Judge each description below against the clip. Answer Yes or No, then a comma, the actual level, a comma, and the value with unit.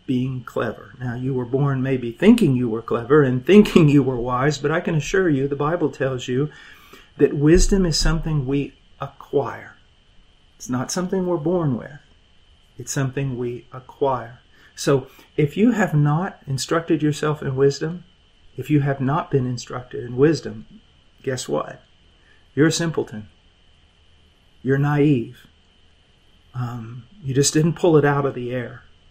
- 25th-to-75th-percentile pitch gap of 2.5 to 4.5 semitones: Yes, average, 4.0 semitones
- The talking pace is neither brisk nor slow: Yes, average, 155 wpm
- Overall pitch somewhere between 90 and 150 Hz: Yes, low, 135 Hz